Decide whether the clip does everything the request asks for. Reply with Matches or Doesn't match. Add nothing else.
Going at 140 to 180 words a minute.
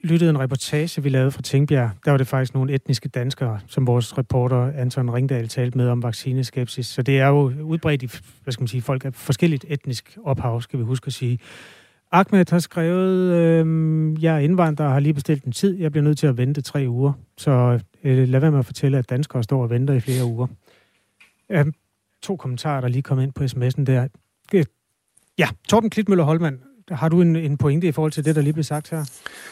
Doesn't match